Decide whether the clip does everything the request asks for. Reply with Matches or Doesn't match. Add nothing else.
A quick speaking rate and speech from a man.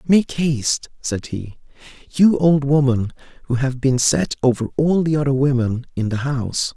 Doesn't match